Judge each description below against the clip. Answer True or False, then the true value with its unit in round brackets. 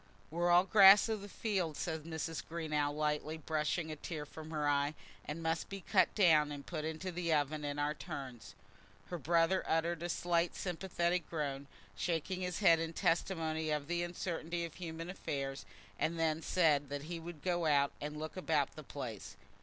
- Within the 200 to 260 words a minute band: False (185 wpm)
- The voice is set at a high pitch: False (160 Hz)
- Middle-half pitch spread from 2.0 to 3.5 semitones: True (2.6 semitones)